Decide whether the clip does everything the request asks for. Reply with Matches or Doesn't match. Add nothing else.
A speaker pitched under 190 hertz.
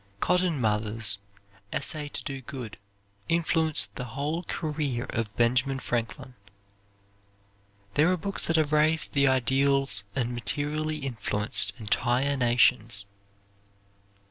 Matches